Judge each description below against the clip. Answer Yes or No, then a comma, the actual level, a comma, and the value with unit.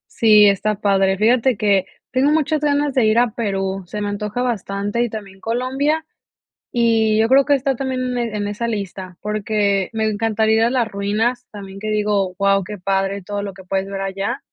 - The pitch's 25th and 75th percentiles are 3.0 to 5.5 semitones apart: Yes, average, 3.3 semitones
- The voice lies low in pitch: No, high, 215 Hz